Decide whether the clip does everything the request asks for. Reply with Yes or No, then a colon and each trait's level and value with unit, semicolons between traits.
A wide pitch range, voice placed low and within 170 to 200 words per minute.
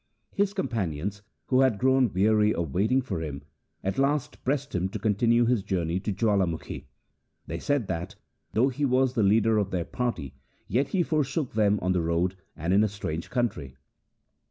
Yes: wide, 5.7 semitones; low, 105 Hz; average, 180 wpm